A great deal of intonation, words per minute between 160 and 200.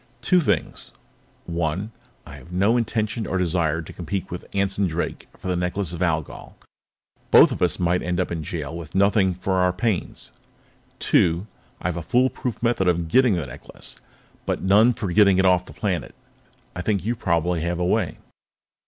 No: average, 3.0 semitones; average, 180 wpm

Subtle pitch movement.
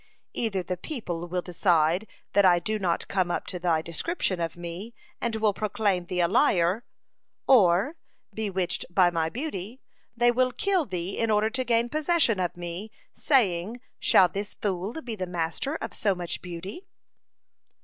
No: average, 4.7 semitones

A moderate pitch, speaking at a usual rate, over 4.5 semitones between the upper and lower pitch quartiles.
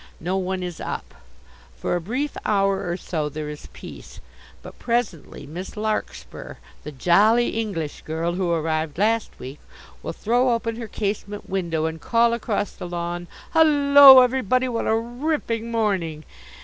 No: high, 200 Hz; average, 150 wpm; wide, 5.5 semitones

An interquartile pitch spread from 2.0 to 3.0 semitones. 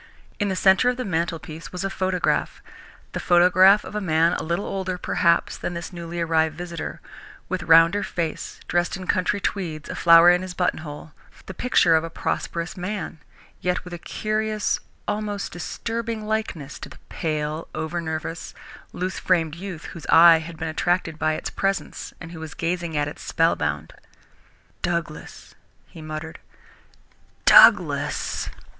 Yes: average, 2.7 semitones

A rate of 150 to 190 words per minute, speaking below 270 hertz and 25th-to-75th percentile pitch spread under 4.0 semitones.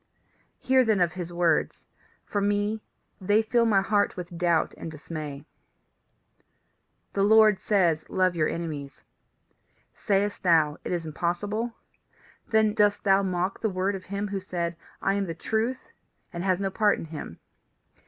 Yes: average, 155 wpm; high, 190 Hz; average, 3.3 semitones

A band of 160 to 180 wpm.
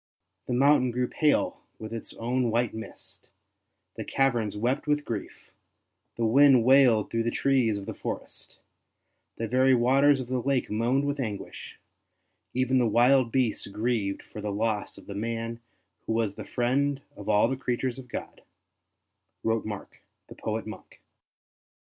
Yes: average, 165 wpm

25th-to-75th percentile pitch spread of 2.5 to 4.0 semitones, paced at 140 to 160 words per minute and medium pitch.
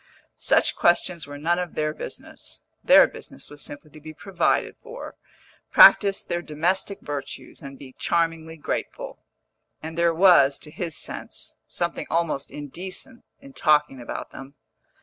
Yes: average, 3.1 semitones; average, 145 wpm; medium, 160 Hz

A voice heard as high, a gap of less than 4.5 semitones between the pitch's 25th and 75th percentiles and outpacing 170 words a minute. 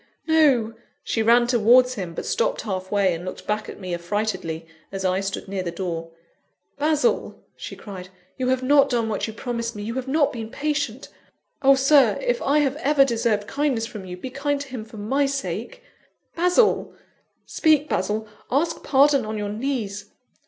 No: high, 235 Hz; average, 5.3 semitones; average, 180 wpm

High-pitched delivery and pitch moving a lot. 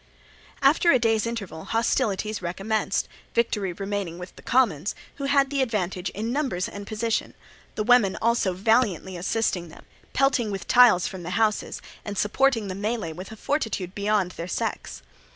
No: high, 210 Hz; average, 3.9 semitones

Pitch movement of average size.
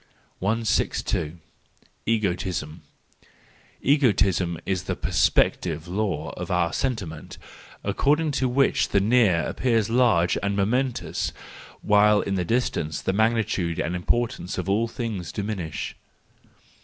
Yes: average, 4.9 semitones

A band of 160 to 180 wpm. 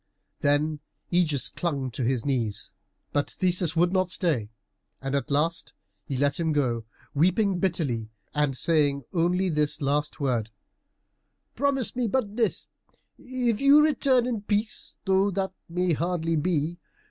No: average, 140 wpm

